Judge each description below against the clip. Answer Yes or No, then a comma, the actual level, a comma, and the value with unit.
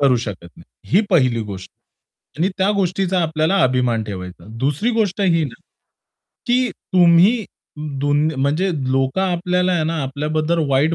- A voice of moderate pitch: Yes, medium, 160 Hz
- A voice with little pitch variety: No, wide, 5.6 semitones